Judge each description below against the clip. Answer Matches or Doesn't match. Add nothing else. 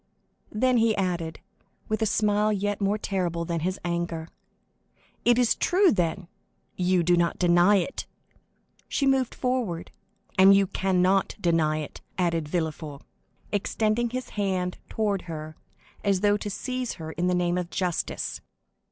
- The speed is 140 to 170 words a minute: Matches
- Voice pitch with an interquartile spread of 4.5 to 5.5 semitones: Doesn't match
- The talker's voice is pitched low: Doesn't match